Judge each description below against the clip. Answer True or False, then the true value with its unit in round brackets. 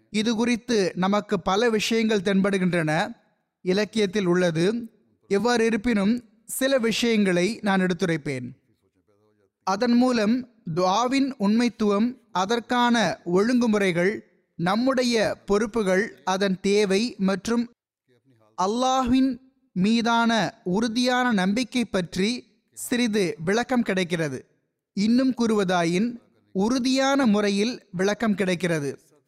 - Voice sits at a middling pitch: False (210 Hz)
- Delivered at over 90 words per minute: False (80 wpm)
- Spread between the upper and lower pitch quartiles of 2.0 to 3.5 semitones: False (4.3 semitones)